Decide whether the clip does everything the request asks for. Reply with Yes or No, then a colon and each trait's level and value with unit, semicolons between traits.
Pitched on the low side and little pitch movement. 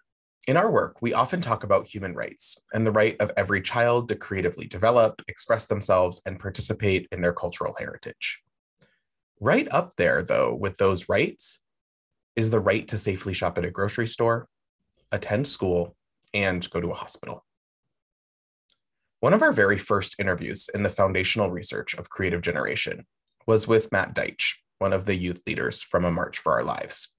No: low, 100 Hz; average, 3.3 semitones